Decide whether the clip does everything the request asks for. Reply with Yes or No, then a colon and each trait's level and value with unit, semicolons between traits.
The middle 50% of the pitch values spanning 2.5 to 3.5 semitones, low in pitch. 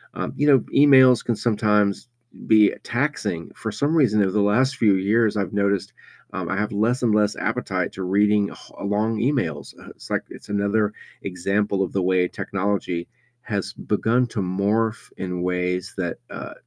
Yes: average, 2.8 semitones; low, 105 Hz